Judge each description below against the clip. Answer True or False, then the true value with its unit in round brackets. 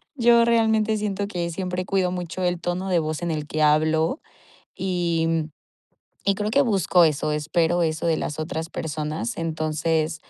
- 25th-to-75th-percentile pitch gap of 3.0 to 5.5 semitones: True (3.5 semitones)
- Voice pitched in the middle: True (170 Hz)